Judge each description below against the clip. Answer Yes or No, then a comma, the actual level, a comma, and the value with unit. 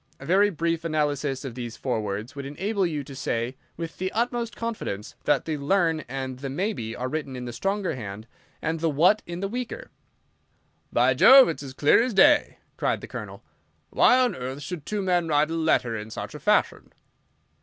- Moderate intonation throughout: No, wide, 6.8 semitones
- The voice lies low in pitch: No, medium, 155 Hz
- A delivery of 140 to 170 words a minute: No, average, 195 wpm